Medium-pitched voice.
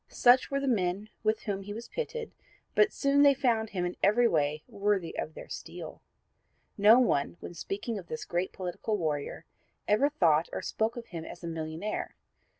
No: high, 205 Hz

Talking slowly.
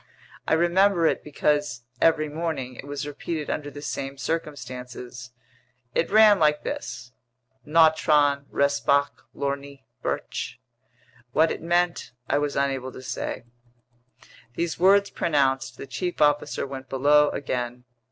Yes: slow, 125 wpm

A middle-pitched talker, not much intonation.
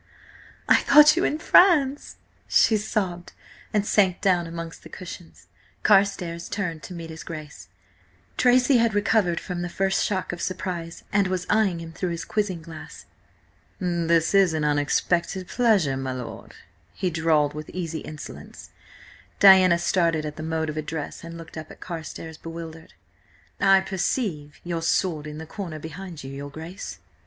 No: medium, 170 Hz; average, 3.3 semitones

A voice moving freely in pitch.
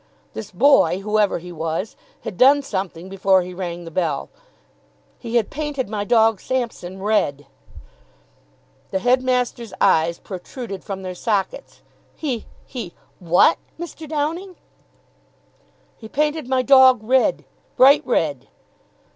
Yes: wide, 6.1 semitones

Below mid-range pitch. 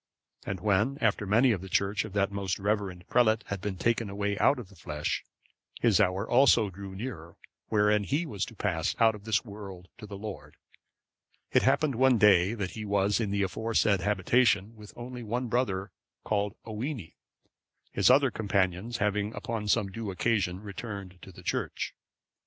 Yes: low, 105 Hz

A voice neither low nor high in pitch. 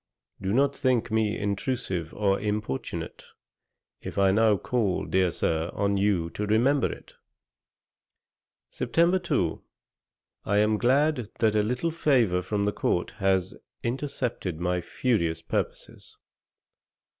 No: low, 105 Hz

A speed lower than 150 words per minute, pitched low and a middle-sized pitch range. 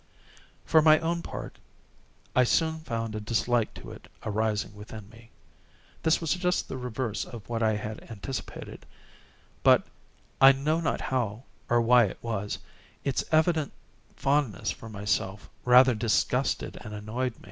Yes: slow, 135 wpm; low, 120 Hz; average, 4.3 semitones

